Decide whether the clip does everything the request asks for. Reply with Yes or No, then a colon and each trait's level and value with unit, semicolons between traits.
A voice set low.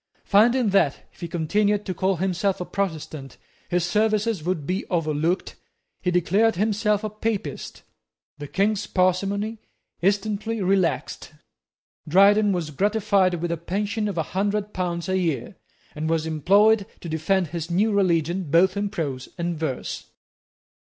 No: high, 190 Hz